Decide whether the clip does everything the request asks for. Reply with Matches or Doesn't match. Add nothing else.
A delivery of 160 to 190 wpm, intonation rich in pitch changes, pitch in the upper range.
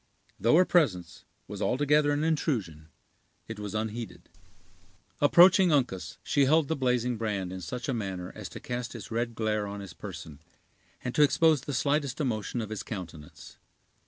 Doesn't match